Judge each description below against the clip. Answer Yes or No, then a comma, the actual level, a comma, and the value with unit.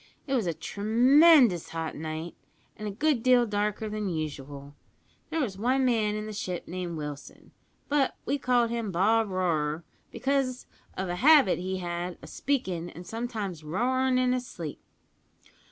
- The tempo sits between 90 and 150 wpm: No, average, 160 wpm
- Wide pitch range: Yes, wide, 6.4 semitones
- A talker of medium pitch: No, high, 210 Hz